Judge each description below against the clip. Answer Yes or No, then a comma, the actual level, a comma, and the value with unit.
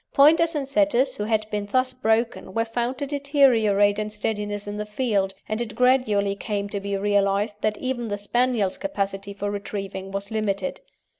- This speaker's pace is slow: No, average, 175 wpm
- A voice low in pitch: No, high, 215 Hz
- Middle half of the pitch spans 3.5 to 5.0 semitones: Yes, average, 3.9 semitones